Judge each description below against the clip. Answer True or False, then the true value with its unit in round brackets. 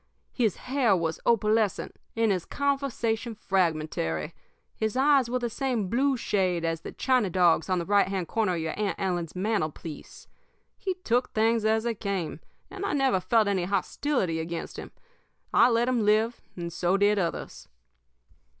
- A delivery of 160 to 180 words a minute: True (165 wpm)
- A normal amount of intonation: True (4.9 semitones)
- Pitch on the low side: False (210 Hz)